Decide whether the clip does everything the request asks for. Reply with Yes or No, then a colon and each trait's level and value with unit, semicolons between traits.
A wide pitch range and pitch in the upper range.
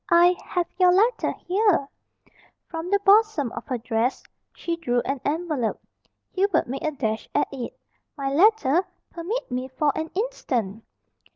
Yes: wide, 6.4 semitones; very high, 320 Hz